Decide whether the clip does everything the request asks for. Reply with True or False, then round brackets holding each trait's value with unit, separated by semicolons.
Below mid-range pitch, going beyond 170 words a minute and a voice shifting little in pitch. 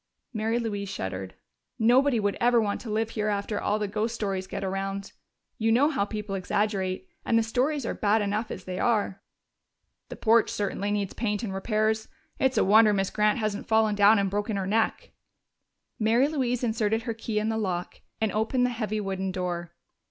False (215 Hz; 190 wpm; 2.2 semitones)